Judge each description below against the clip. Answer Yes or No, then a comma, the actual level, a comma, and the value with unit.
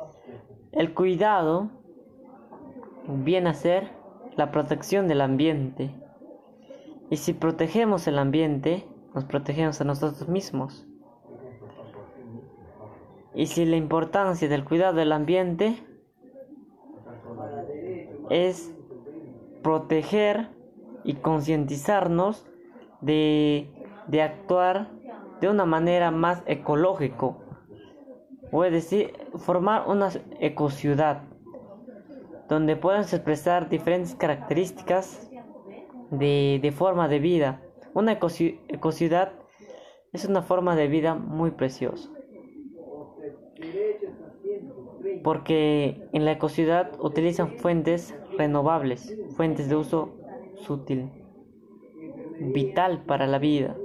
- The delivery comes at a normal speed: No, slow, 90 wpm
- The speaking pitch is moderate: Yes, medium, 165 Hz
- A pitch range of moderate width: Yes, average, 4.3 semitones